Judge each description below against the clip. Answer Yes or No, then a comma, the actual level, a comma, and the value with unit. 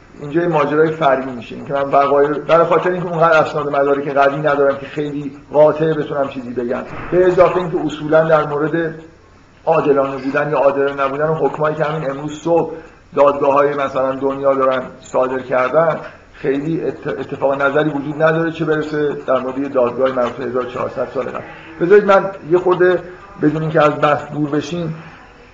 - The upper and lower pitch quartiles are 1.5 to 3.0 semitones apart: Yes, narrow, 2.5 semitones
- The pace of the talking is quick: Yes, fast, 170 wpm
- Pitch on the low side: No, medium, 150 Hz